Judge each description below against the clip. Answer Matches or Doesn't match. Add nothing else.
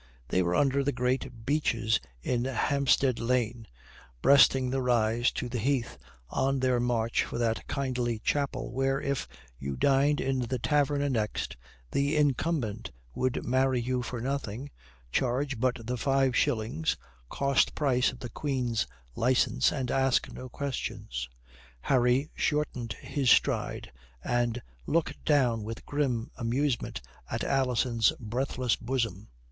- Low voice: Matches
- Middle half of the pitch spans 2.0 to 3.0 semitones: Matches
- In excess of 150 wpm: Doesn't match